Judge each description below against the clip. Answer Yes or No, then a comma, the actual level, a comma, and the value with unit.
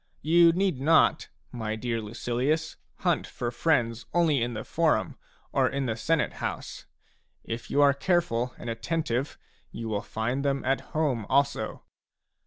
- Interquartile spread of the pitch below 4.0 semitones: No, average, 5.1 semitones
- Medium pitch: No, low, 130 Hz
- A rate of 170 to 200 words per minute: No, average, 150 wpm